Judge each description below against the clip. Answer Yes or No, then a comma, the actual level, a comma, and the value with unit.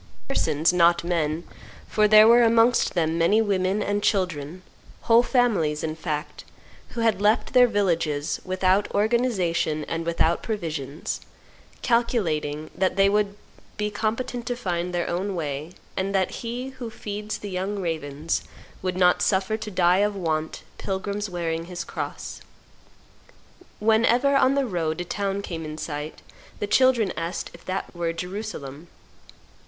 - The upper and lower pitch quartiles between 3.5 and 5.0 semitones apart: Yes, average, 4.4 semitones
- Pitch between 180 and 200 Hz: Yes, medium, 185 Hz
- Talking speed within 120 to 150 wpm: Yes, average, 145 wpm